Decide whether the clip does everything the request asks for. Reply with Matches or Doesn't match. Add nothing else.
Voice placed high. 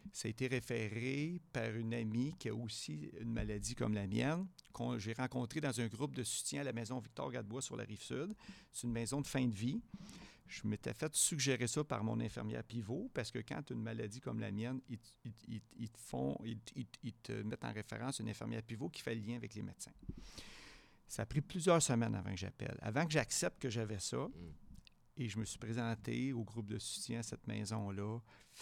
Doesn't match